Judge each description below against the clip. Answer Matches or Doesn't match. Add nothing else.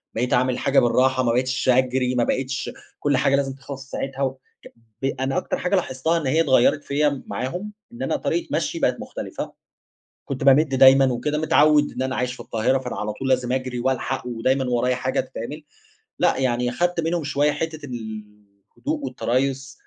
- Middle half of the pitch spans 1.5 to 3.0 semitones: Matches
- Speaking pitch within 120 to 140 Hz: Matches